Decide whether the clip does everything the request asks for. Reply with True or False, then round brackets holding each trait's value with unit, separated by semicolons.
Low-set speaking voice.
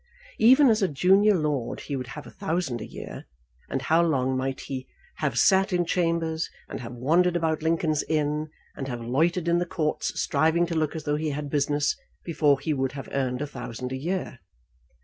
False (155 Hz)